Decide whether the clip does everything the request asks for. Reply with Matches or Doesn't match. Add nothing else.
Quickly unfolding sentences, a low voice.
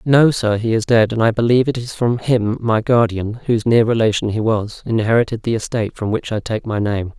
Matches